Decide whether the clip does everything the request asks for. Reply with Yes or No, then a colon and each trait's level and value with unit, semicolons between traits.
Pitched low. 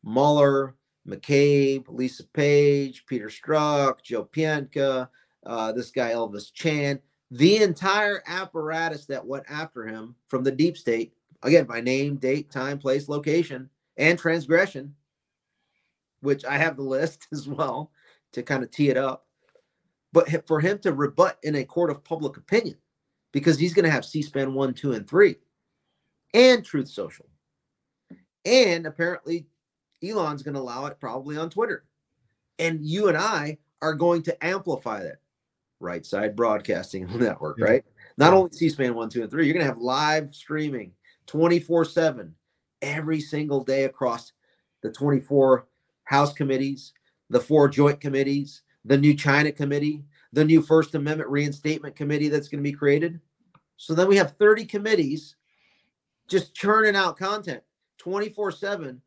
No: medium, 145 Hz